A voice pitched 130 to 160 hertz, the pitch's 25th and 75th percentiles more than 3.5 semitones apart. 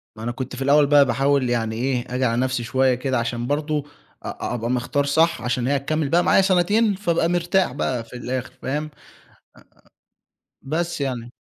Yes: low, 135 Hz; average, 3.9 semitones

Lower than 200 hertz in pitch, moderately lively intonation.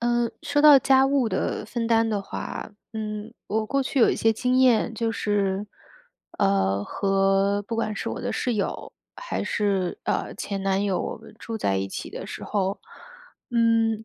No: high, 215 Hz; average, 3.0 semitones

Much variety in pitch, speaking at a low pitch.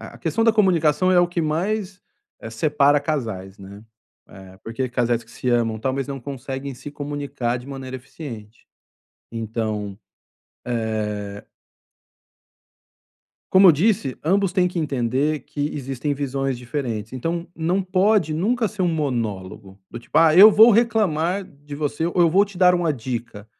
No: wide, 6.8 semitones; medium, 145 Hz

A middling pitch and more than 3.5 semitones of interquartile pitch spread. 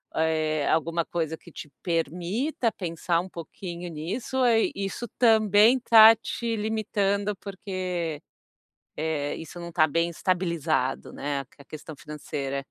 Yes: medium, 170 Hz; average, 4.7 semitones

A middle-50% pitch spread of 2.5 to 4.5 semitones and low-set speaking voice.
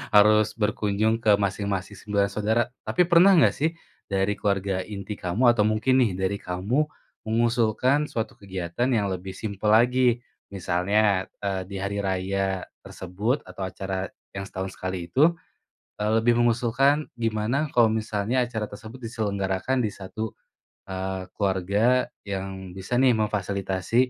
Yes: average, 3.5 semitones; low, 105 Hz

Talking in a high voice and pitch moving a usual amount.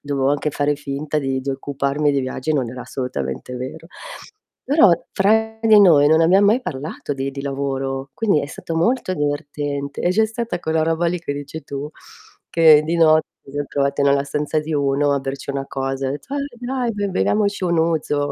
No: medium, 145 Hz; average, 3.6 semitones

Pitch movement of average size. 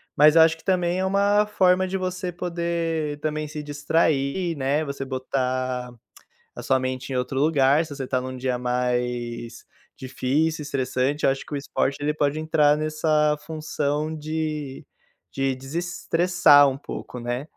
Yes: average, 3.5 semitones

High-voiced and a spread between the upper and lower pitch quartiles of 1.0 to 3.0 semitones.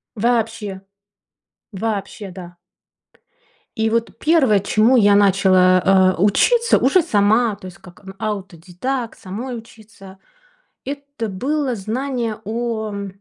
No: high, 215 Hz; average, 3.7 semitones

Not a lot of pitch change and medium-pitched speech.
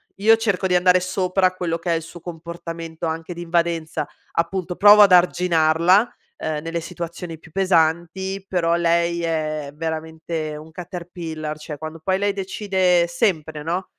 Yes: narrow, 2.2 semitones; medium, 170 Hz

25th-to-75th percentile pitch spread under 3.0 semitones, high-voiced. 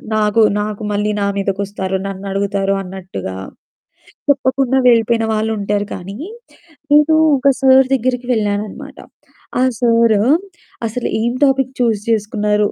No: average, 3.3 semitones; high, 215 Hz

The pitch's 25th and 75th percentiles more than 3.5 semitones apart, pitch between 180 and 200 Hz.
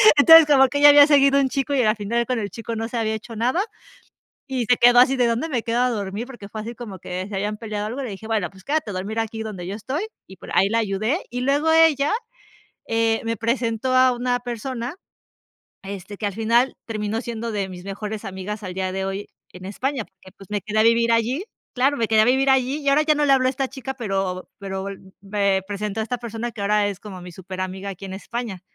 No: average, 4.2 semitones; high, 225 Hz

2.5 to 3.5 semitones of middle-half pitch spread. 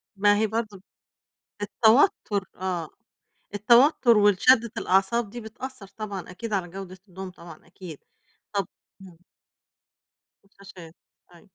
Yes: average, 3.0 semitones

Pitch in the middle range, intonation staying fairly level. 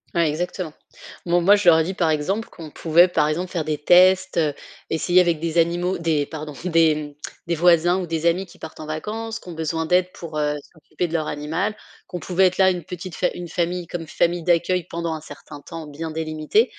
Yes: medium, 170 Hz; narrow, 2.3 semitones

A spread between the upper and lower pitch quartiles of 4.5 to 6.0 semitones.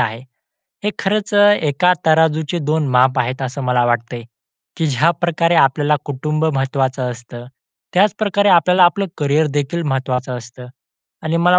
Yes: average, 4.8 semitones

